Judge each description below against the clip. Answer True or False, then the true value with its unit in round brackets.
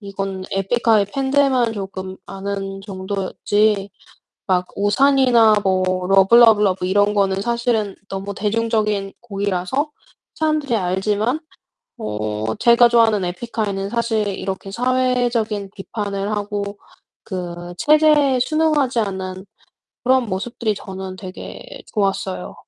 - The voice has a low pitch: False (205 Hz)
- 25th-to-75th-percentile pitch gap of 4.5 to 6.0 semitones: False (3.6 semitones)